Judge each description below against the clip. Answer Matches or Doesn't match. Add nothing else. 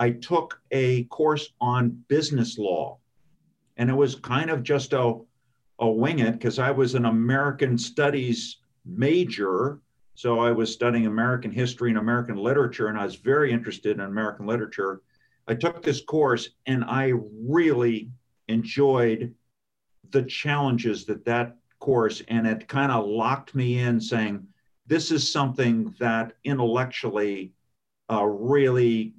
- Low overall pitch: Matches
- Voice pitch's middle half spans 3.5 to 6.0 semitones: Doesn't match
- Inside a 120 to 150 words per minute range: Matches